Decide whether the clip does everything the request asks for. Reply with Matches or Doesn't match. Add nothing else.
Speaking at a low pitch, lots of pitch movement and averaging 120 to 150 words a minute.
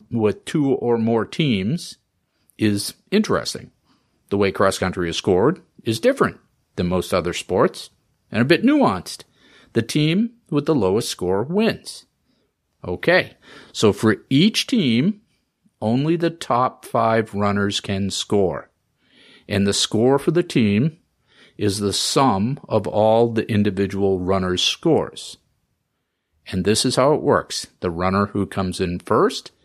Matches